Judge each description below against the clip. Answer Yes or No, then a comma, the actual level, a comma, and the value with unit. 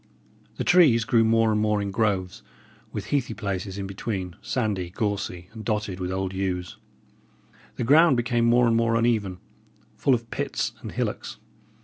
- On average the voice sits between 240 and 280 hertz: No, low, 110 Hz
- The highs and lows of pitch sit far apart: No, average, 3.5 semitones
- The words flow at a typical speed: Yes, average, 160 wpm